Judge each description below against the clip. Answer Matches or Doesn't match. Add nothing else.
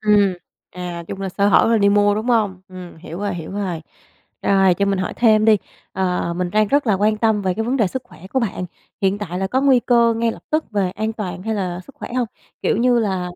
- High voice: Matches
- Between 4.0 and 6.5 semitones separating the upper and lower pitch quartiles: Doesn't match